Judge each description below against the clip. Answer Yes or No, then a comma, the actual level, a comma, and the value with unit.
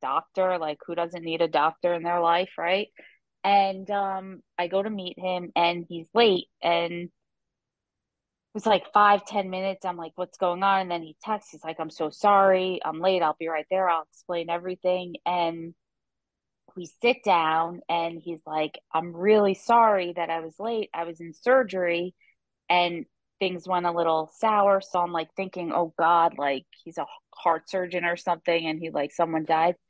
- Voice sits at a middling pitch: Yes, medium, 175 Hz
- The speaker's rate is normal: Yes, average, 185 wpm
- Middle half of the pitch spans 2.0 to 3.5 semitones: Yes, narrow, 2.4 semitones